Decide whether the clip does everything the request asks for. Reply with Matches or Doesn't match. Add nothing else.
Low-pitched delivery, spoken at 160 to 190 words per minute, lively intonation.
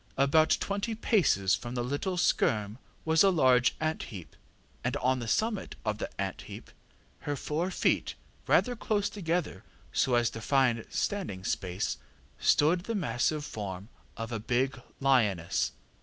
Doesn't match